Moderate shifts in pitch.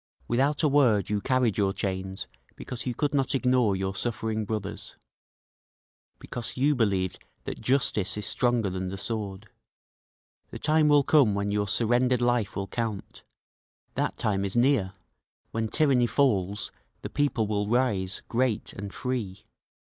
Yes: average, 4.4 semitones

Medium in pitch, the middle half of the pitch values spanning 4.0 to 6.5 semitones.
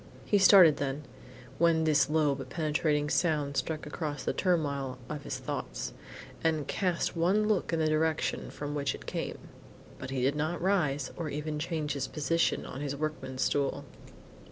No: medium, 150 Hz; narrow, 2.5 semitones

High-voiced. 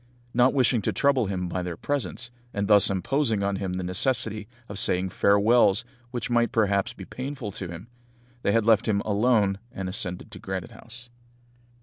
No: low, 105 Hz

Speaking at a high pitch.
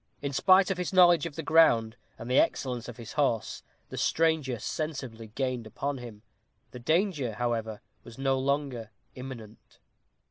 No: low, 130 Hz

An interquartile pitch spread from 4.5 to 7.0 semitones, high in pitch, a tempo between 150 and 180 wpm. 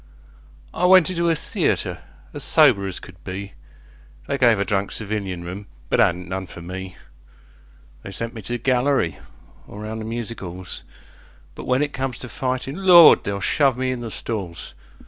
No: wide, 5.6 semitones; low, 110 Hz; average, 165 wpm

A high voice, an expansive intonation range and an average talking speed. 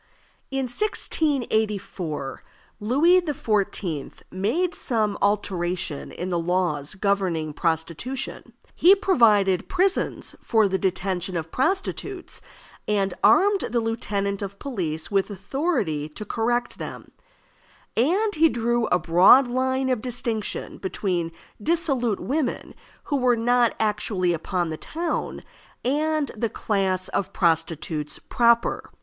No: high, 210 Hz; wide, 6.1 semitones; slow, 115 wpm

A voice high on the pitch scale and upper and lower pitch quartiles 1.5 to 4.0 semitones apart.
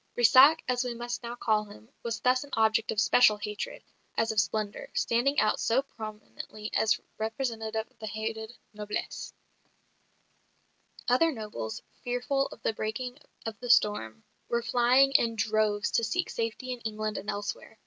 Yes: high, 225 Hz; narrow, 2.4 semitones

